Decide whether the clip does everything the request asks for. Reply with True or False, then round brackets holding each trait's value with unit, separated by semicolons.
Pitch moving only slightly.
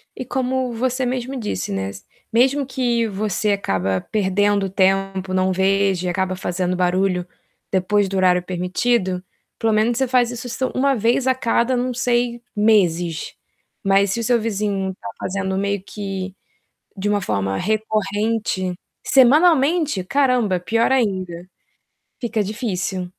False (4.2 semitones)